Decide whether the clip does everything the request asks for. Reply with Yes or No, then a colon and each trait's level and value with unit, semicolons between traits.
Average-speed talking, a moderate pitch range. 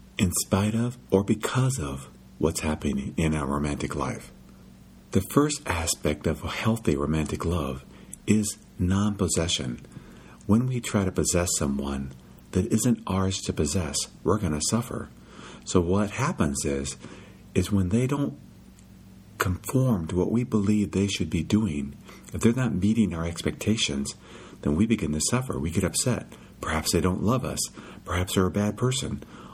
No: average, 160 wpm; wide, 6.3 semitones